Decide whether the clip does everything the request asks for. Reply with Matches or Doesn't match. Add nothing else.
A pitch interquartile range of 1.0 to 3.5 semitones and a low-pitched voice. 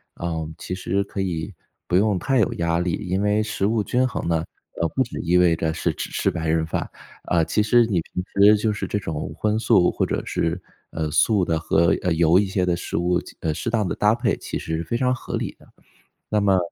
Doesn't match